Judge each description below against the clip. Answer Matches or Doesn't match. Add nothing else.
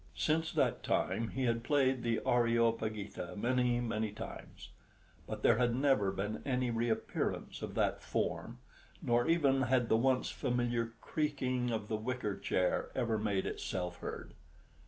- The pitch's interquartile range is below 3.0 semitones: Matches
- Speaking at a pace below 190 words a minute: Matches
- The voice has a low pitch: Matches